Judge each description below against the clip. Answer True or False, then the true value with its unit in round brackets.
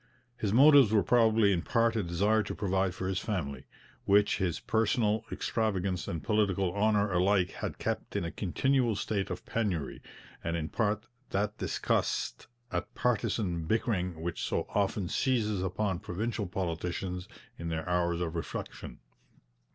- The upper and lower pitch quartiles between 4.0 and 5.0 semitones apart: False (3.6 semitones)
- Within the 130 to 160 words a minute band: True (150 wpm)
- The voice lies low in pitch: True (100 Hz)